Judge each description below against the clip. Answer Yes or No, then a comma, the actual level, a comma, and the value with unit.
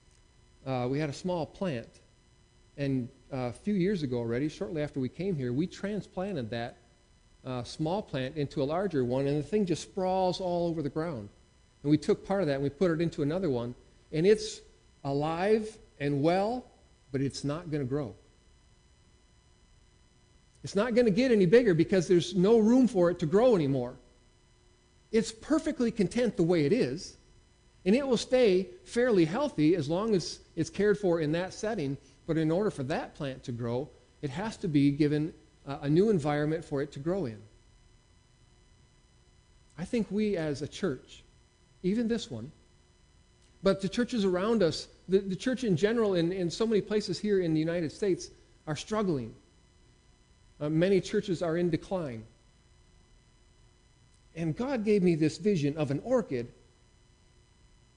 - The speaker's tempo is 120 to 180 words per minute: Yes, average, 170 wpm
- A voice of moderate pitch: Yes, medium, 160 Hz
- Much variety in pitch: Yes, wide, 7.2 semitones